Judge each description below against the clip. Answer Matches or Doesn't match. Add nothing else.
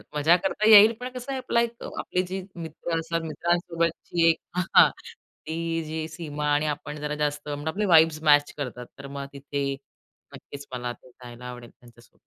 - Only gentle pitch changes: Doesn't match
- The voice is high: Doesn't match